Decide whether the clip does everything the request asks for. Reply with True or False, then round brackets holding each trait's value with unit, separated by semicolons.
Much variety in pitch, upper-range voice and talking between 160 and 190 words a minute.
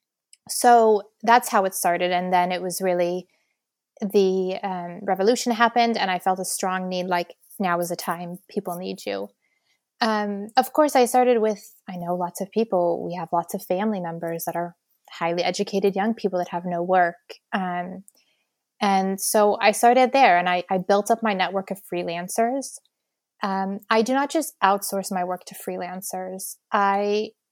False (3.3 semitones; 195 Hz; 175 wpm)